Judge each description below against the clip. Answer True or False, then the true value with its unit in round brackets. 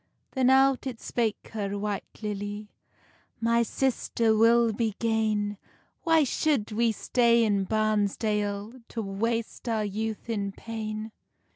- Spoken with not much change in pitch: True (2.0 semitones)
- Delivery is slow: True (125 wpm)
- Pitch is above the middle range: True (220 Hz)